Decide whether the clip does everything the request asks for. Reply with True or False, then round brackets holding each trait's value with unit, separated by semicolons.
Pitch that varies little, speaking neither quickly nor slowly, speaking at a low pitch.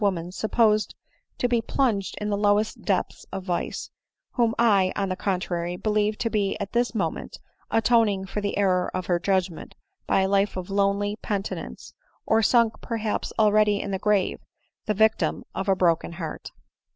False (2.3 semitones; 175 wpm; 205 Hz)